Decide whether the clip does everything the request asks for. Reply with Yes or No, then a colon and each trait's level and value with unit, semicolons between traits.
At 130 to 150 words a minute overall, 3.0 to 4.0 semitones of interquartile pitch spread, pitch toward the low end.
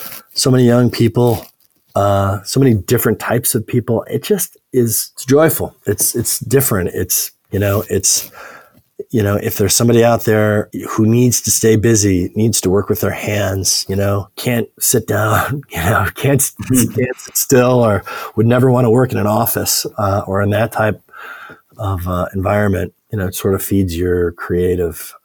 No: average, 185 wpm; average, 3.3 semitones; low, 105 Hz